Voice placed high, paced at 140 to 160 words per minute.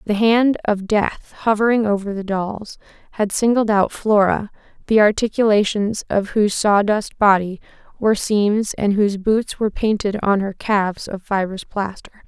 Yes: high, 205 Hz; average, 150 wpm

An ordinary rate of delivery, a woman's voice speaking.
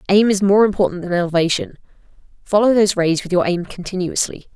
Yes: average, 170 wpm; female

